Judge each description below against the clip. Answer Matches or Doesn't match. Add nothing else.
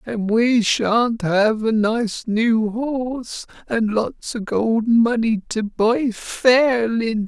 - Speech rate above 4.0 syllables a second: Doesn't match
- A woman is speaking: Doesn't match